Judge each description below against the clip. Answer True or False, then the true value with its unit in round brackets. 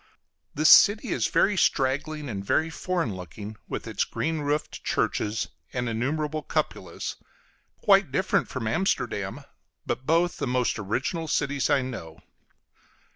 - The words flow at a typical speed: False (130 wpm)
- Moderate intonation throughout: False (5.8 semitones)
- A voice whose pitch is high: False (140 Hz)